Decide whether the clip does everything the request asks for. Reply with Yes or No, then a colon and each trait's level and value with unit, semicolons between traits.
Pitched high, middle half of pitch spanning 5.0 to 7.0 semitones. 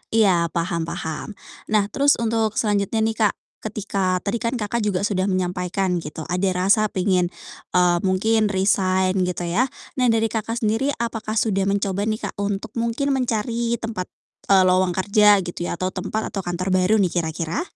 No: high, 200 Hz; average, 3.2 semitones